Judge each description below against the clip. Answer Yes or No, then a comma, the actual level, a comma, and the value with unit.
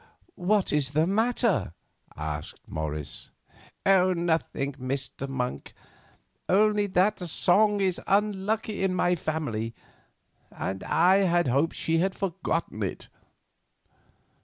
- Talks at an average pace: No, slow, 105 wpm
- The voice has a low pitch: No, medium, 175 Hz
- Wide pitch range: Yes, wide, 6.3 semitones